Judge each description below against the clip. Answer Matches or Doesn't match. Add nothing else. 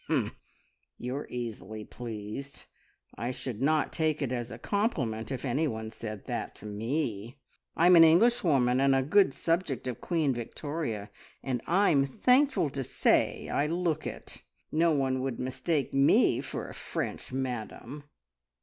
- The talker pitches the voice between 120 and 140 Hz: Matches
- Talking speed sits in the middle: Matches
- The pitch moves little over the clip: Doesn't match